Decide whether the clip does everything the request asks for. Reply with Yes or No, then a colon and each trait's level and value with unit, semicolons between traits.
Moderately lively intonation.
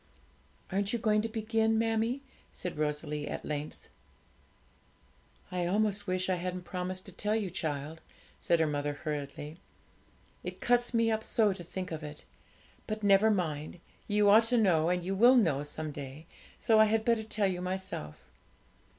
No: wide, 5.7 semitones